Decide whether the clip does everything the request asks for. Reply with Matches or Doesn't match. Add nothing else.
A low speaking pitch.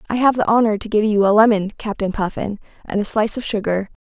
Doesn't match